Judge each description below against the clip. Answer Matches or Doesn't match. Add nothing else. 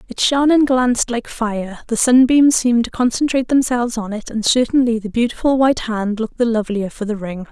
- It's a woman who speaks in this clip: Matches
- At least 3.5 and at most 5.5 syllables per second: Doesn't match